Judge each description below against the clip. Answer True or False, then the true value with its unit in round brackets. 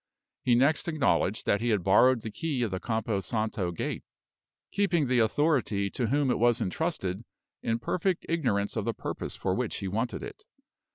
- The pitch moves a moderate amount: False (5.8 semitones)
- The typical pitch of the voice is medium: False (120 Hz)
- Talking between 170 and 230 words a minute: True (180 wpm)